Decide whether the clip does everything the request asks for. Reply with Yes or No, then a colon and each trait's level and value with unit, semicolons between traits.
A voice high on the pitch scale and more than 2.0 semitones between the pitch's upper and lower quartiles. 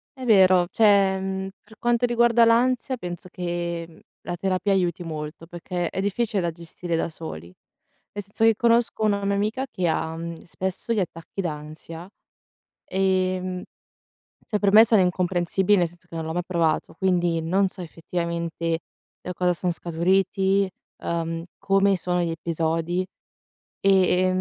No: medium, 180 Hz; average, 2.8 semitones